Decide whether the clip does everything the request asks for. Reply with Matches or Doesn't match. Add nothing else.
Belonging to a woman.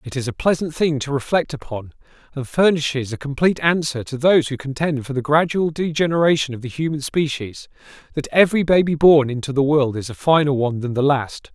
Doesn't match